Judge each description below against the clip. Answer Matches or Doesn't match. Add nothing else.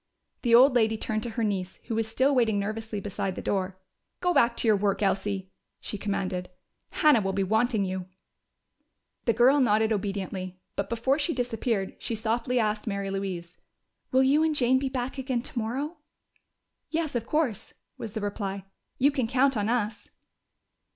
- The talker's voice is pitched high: Matches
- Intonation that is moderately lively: Matches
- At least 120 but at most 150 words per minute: Doesn't match